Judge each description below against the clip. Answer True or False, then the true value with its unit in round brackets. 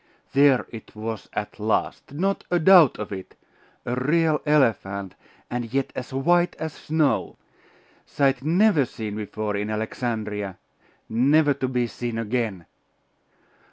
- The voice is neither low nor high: False (125 Hz)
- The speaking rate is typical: False (130 wpm)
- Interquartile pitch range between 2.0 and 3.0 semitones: False (5.6 semitones)